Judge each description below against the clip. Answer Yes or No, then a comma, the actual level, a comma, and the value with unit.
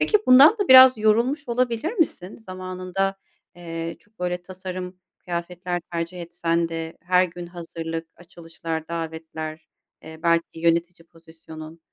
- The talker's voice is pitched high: No, medium, 175 Hz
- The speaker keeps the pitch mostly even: Yes, narrow, 2.3 semitones